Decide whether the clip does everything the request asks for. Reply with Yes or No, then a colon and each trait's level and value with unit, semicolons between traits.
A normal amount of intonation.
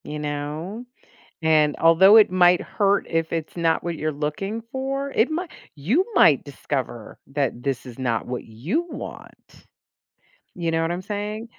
No: wide, 6.0 semitones